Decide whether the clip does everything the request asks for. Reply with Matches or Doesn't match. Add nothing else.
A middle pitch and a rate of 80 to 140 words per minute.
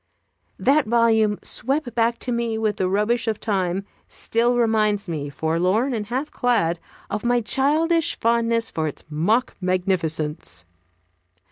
Doesn't match